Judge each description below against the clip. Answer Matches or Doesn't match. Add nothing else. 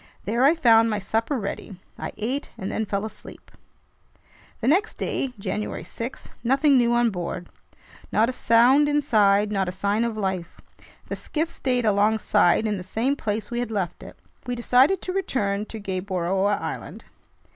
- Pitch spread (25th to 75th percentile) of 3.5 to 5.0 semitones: Matches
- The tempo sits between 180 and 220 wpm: Doesn't match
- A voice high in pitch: Matches